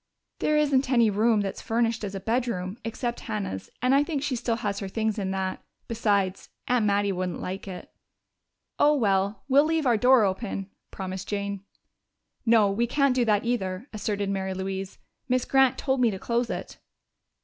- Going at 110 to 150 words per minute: No, average, 180 wpm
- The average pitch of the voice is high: Yes, high, 220 Hz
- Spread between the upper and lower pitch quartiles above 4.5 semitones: No, average, 4.0 semitones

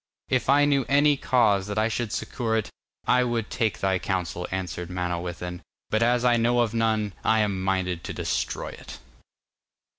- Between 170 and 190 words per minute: Yes, average, 175 wpm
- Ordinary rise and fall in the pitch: Yes, average, 4.4 semitones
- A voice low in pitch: Yes, low, 110 Hz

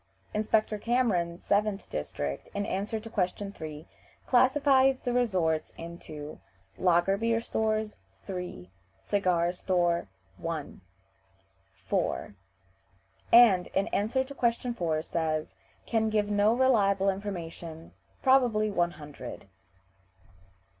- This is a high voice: Yes, high, 200 Hz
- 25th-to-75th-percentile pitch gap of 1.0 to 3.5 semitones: No, average, 4.9 semitones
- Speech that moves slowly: Yes, slow, 105 wpm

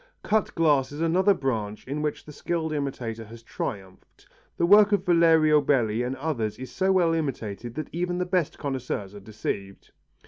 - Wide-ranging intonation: Yes, wide, 6.6 semitones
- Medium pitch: Yes, medium, 145 Hz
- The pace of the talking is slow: No, average, 175 wpm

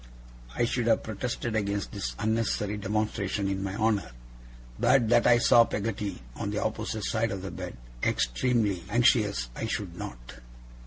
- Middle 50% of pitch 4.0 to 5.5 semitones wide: No, average, 2.8 semitones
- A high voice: No, low, 105 Hz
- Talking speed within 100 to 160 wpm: Yes, average, 155 wpm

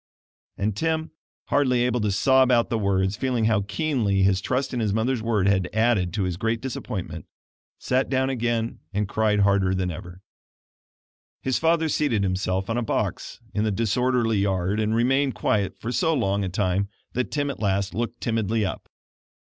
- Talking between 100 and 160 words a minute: No, average, 175 wpm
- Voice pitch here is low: Yes, low, 110 Hz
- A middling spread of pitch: Yes, average, 4.1 semitones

